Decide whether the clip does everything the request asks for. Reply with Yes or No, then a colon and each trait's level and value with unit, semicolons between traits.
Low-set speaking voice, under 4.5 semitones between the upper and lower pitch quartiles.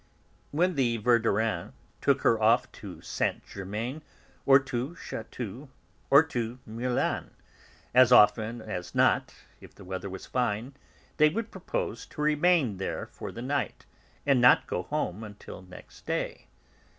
No: low, 120 Hz; average, 4.8 semitones